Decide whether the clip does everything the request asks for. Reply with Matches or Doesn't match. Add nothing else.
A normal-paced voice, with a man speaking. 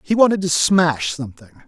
Matches